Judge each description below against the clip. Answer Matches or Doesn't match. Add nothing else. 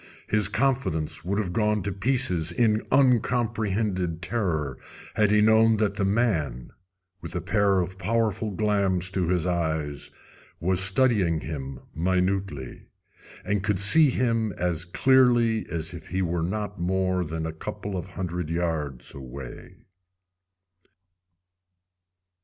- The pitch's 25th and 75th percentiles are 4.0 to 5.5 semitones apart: Matches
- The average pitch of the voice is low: Matches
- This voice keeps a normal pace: Doesn't match